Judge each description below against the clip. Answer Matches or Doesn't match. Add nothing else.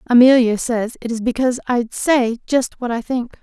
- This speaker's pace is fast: Doesn't match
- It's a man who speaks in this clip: Doesn't match